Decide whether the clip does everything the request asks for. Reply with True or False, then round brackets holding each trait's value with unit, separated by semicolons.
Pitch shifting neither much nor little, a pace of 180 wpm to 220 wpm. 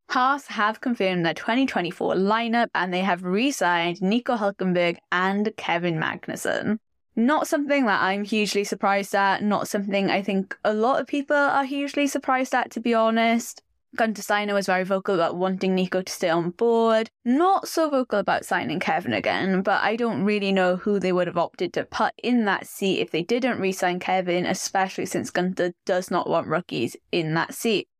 True (4.2 semitones; 190 wpm)